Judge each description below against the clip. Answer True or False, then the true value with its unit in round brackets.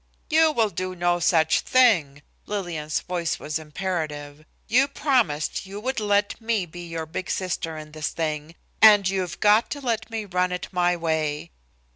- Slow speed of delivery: False (165 wpm)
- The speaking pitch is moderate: True (180 Hz)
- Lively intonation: False (4.9 semitones)